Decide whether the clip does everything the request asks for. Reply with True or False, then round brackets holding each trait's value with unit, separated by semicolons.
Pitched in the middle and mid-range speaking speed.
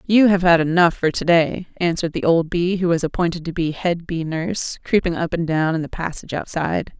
False (170 Hz; 230 wpm)